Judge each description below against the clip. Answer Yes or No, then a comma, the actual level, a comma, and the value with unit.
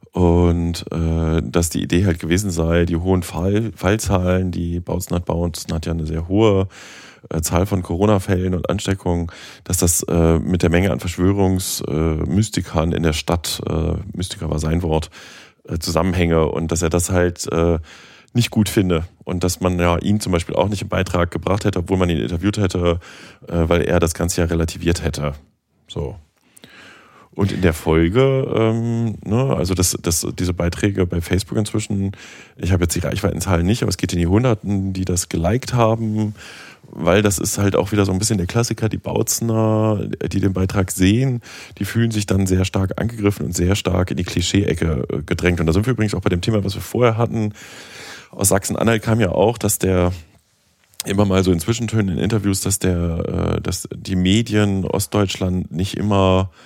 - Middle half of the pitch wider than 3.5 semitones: No, average, 3.1 semitones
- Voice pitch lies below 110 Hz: Yes, very low, 95 Hz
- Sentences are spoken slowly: No, fast, 190 wpm